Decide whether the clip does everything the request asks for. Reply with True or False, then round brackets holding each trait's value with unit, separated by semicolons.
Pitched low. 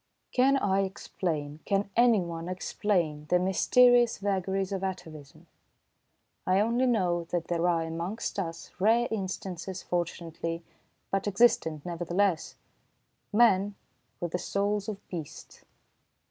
False (185 Hz)